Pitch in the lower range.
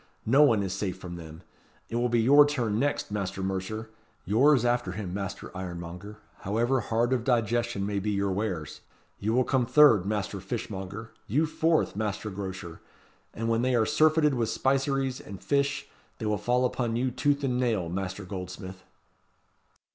Yes: low, 110 Hz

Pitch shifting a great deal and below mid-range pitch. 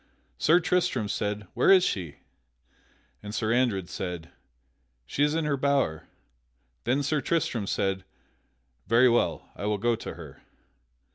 Yes: wide, 5.9 semitones; low, 120 Hz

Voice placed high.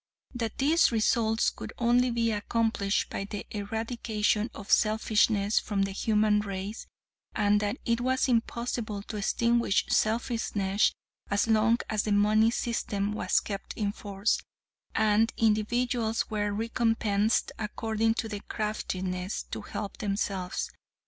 Yes: high, 215 Hz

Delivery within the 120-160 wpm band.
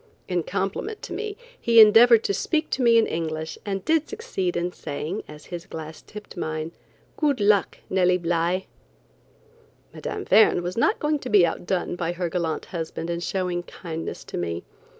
No: average, 170 wpm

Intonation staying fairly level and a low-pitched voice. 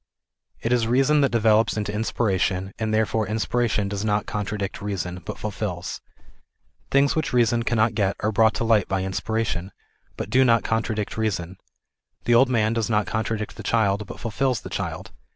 Yes: narrow, 2.3 semitones; low, 110 Hz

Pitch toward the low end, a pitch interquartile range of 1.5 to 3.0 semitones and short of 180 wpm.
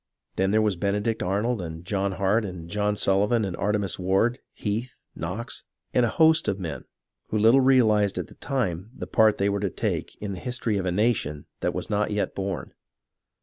No: low, 105 Hz; average, 2.7 semitones; average, 195 wpm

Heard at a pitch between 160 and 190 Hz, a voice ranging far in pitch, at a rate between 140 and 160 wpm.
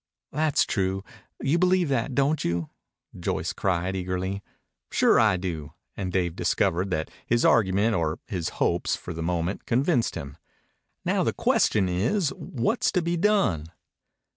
No: very low, 95 Hz; wide, 7.7 semitones; average, 150 wpm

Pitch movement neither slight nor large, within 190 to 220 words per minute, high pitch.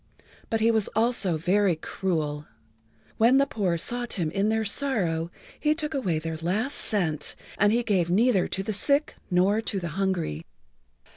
No: average, 5.0 semitones; average, 165 wpm; high, 195 Hz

